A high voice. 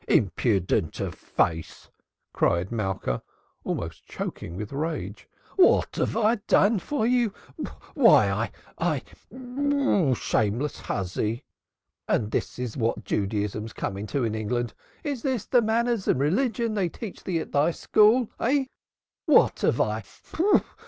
No: medium, 145 Hz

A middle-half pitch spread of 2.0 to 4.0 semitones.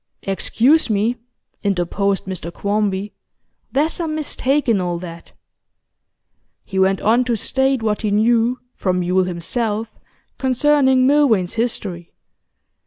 No: average, 5.2 semitones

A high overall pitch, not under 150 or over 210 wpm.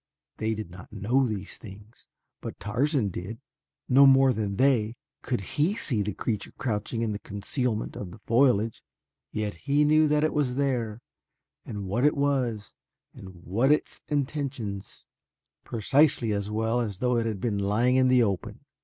No: low, 115 Hz; average, 165 wpm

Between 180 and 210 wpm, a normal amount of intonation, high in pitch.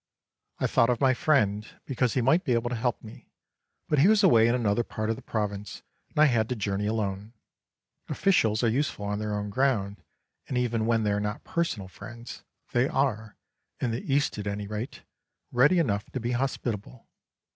No: average, 195 wpm; average, 3.7 semitones; low, 115 Hz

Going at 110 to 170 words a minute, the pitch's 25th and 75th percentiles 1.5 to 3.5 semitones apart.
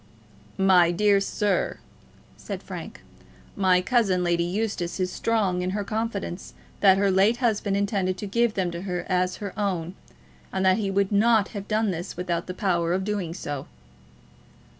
Yes: average, 165 wpm; narrow, 2.4 semitones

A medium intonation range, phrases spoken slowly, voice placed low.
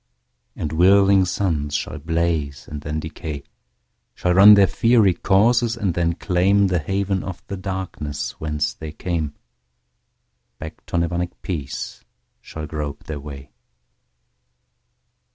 Yes: average, 4.1 semitones; slow, 115 wpm; very low, 85 Hz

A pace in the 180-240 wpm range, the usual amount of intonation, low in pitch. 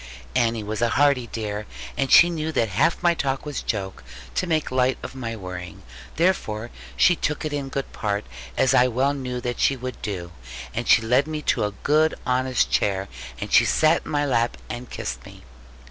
Yes: average, 200 wpm; average, 4.8 semitones; low, 125 Hz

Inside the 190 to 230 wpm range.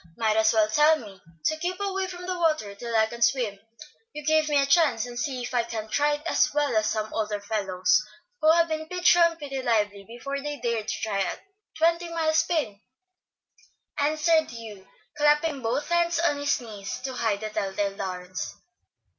Yes: average, 195 wpm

